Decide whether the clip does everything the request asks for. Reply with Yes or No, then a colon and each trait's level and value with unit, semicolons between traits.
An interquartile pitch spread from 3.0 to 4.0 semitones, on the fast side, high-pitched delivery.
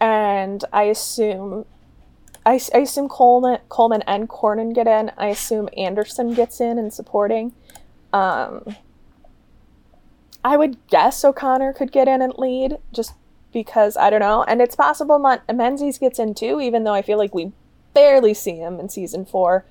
No: average, 3.6 semitones; average, 165 wpm; high, 230 Hz